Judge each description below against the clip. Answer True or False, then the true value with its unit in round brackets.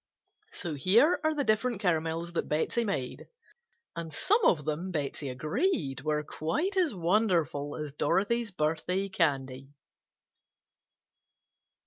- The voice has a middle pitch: True (170 Hz)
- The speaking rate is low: True (115 wpm)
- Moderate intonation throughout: False (6.3 semitones)